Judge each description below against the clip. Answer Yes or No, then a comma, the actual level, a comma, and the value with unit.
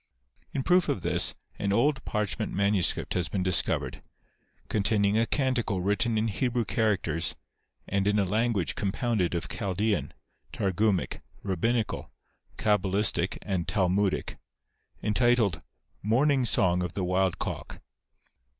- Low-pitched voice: Yes, low, 100 Hz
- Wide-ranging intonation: No, average, 3.4 semitones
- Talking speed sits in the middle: No, slow, 125 wpm